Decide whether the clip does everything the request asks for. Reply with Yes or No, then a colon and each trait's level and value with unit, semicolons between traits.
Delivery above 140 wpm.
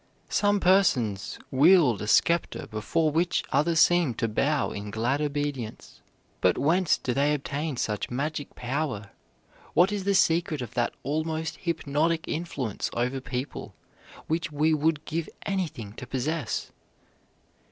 No: slow, 135 wpm